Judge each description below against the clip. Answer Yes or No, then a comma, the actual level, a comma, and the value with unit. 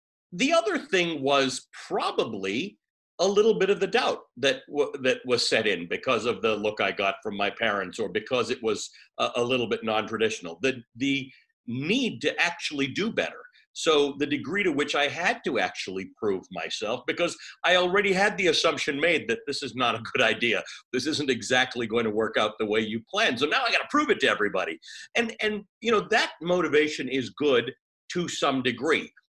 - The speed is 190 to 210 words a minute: Yes, average, 200 wpm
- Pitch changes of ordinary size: No, wide, 8.6 semitones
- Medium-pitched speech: Yes, medium, 150 Hz